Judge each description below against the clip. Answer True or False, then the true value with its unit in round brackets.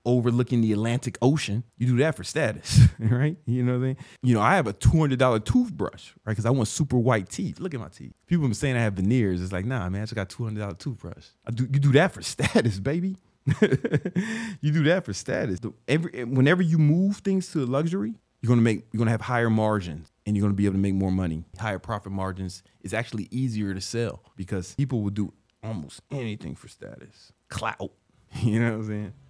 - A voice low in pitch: True (115 Hz)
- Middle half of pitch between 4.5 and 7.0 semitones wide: True (4.9 semitones)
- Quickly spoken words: True (230 wpm)